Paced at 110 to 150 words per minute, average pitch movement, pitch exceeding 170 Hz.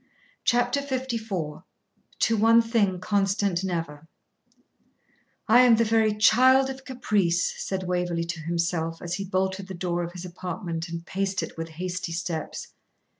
Yes: average, 145 wpm; average, 4.7 semitones; medium, 185 Hz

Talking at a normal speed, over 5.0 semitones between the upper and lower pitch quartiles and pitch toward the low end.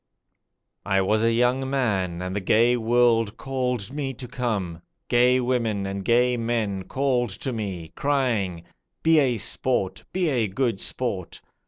No: average, 150 wpm; average, 4.3 semitones; low, 115 Hz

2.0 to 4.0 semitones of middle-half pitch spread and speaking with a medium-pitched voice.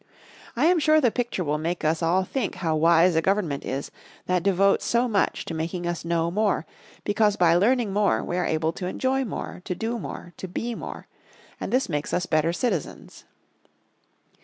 No: average, 5.0 semitones; medium, 180 Hz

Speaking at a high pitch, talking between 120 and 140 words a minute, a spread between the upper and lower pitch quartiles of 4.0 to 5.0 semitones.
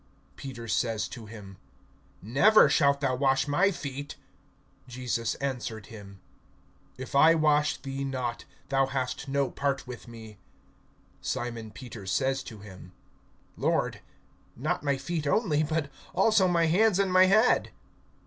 No: low, 135 Hz; slow, 135 wpm; average, 4.5 semitones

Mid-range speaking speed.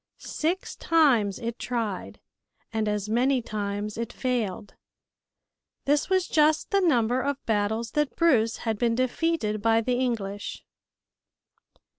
No: slow, 125 wpm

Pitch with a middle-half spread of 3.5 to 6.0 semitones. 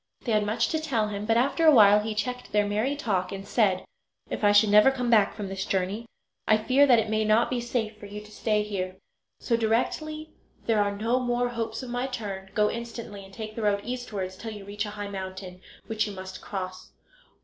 No: average, 2.7 semitones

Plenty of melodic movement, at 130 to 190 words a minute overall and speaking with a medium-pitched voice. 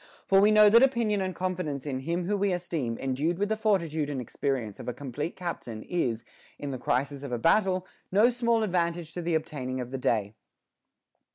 No: wide, 6.5 semitones; fast, 205 wpm; medium, 165 Hz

